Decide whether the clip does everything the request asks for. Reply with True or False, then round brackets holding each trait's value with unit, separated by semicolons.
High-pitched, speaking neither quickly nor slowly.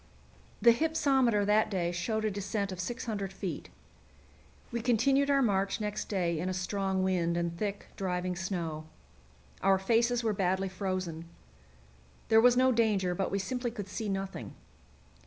True (195 Hz; 155 wpm)